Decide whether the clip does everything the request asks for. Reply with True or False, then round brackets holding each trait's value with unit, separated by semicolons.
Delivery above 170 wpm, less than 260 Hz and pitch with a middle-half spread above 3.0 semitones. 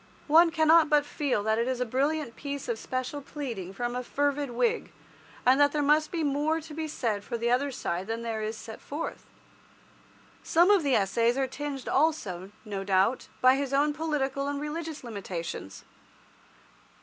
False (180 wpm; 275 Hz; 4.5 semitones)